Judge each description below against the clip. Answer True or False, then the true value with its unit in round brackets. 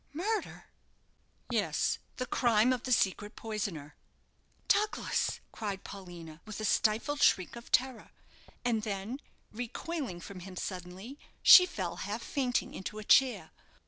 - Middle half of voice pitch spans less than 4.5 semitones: False (4.9 semitones)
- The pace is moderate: False (130 wpm)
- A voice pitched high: True (215 Hz)